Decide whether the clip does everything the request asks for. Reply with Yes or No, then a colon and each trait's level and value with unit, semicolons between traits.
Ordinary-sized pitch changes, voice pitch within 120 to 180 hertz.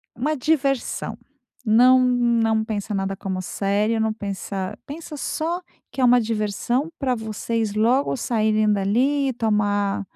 No: average, 3.6 semitones; high, 225 Hz